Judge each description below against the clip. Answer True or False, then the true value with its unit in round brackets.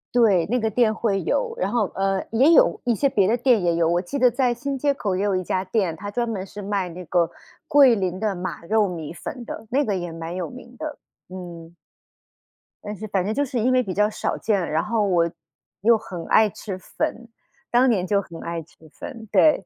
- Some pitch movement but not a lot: True (4.8 semitones)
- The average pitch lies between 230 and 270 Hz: False (205 Hz)